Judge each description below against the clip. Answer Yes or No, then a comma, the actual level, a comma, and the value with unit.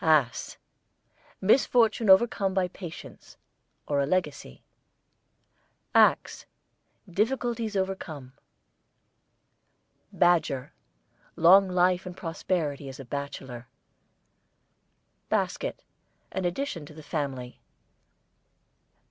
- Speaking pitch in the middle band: Yes, medium, 175 Hz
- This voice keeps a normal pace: No, slow, 80 wpm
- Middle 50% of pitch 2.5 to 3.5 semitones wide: No, average, 5.2 semitones